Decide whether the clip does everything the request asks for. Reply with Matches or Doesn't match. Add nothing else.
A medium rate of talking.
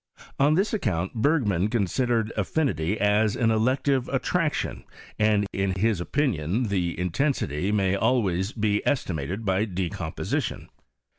Doesn't match